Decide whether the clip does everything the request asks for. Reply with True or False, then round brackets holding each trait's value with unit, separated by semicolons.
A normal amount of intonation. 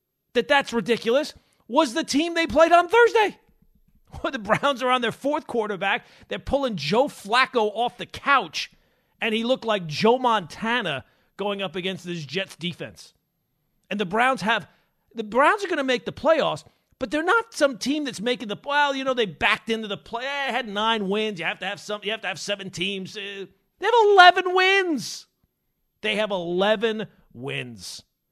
False (5.9 semitones)